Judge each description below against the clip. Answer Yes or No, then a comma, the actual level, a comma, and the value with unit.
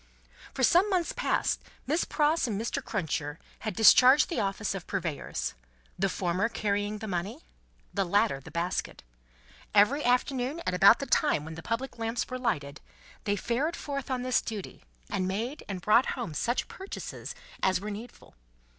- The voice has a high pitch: Yes, high, 215 Hz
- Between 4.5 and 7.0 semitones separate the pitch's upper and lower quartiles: Yes, average, 5.2 semitones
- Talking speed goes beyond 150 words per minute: Yes, average, 165 wpm